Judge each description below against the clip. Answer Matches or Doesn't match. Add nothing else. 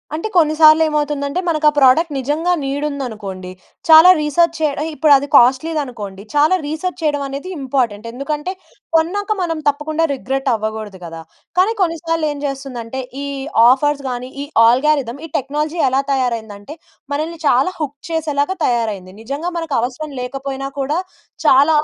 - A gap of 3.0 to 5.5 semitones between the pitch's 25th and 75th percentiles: Matches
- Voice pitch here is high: Matches